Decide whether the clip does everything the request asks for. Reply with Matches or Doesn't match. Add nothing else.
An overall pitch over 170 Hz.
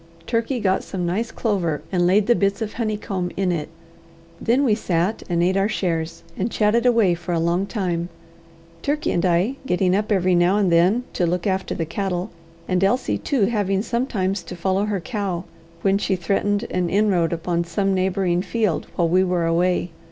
Matches